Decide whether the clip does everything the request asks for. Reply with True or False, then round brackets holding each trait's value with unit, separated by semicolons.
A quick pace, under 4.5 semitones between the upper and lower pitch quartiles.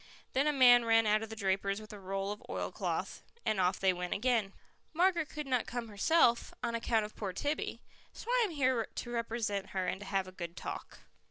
True (220 wpm; 4.1 semitones)